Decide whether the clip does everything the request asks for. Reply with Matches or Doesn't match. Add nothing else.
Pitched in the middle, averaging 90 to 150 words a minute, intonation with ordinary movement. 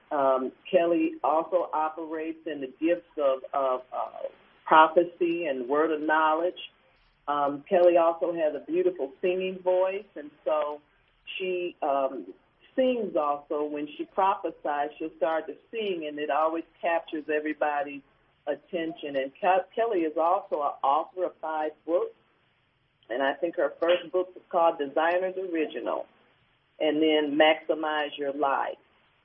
Matches